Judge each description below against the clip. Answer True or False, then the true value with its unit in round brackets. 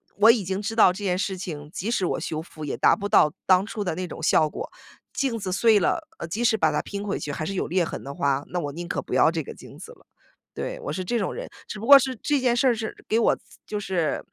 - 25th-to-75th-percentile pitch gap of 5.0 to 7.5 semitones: True (5.3 semitones)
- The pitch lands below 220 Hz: True (195 Hz)